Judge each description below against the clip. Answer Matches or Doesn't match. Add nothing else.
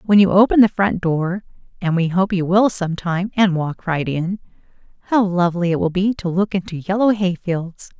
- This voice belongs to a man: Doesn't match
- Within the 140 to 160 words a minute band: Doesn't match